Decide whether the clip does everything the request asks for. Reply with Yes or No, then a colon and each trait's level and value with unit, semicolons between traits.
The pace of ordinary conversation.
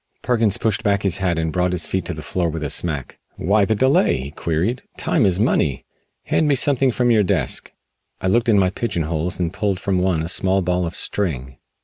No: fast, 220 wpm